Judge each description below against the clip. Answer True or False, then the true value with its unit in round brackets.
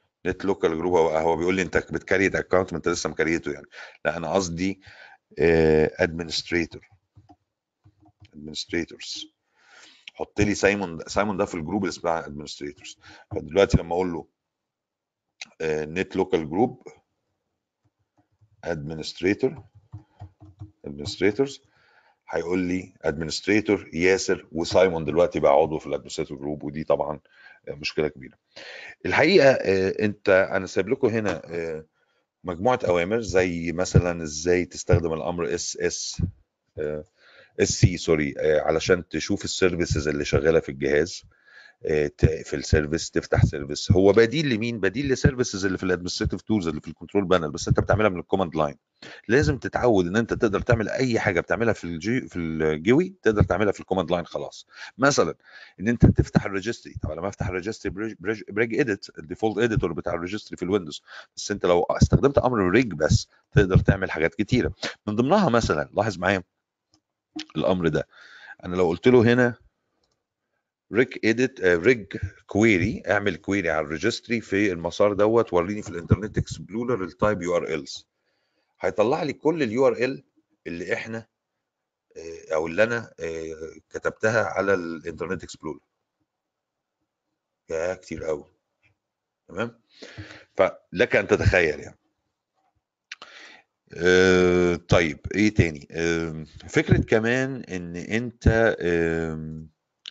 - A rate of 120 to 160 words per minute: True (130 wpm)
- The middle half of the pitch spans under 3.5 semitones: False (4.6 semitones)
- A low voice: True (95 Hz)